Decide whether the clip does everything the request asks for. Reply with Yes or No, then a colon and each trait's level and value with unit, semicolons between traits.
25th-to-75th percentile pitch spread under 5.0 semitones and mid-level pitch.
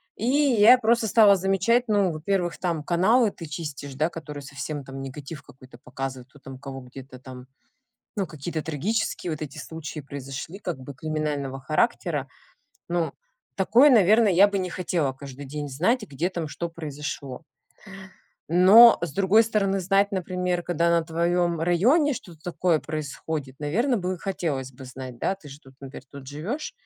No: wide, 5.6 semitones; medium, 165 Hz